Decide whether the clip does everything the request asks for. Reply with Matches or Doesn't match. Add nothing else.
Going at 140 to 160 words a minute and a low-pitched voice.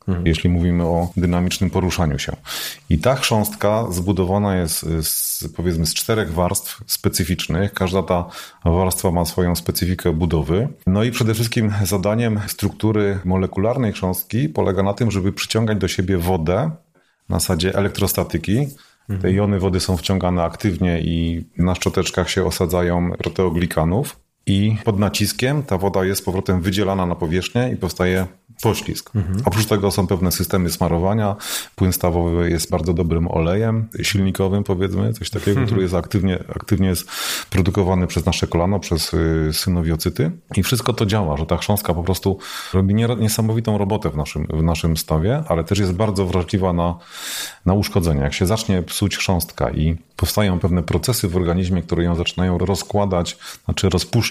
Matches